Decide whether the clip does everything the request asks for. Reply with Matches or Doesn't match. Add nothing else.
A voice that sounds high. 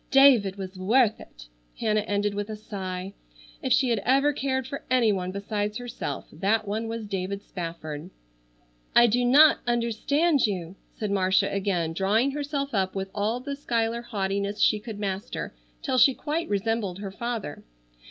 Matches